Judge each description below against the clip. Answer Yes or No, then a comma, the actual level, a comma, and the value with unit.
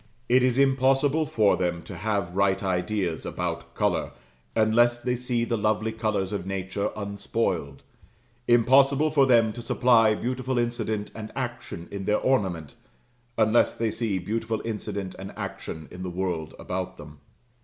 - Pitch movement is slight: No, average, 4.0 semitones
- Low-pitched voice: Yes, low, 110 Hz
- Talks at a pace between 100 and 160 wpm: Yes, average, 150 wpm